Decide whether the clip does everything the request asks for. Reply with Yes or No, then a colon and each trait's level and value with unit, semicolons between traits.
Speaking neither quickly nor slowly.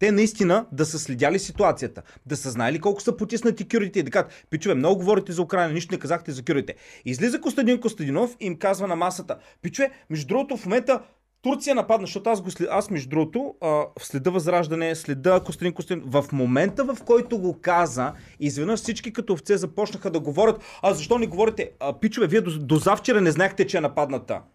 No: fast, 195 wpm